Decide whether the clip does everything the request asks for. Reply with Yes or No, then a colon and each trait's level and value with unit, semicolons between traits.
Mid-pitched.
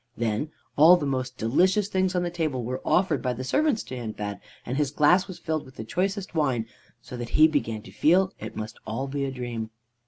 Yes: medium, 145 Hz